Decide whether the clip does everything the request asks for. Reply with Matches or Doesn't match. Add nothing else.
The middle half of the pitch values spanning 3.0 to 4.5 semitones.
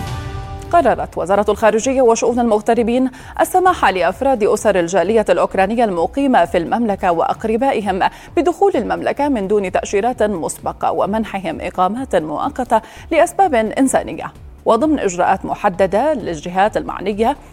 Doesn't match